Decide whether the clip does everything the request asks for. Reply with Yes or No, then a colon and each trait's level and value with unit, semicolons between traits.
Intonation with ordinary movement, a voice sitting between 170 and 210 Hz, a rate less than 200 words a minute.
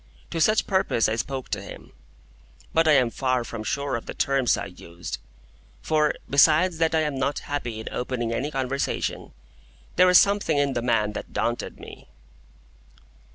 No: average, 4.7 semitones; low, 135 Hz; average, 170 wpm